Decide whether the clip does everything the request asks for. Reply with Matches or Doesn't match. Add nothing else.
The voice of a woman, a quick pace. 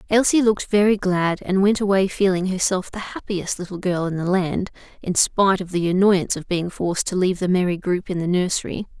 Matches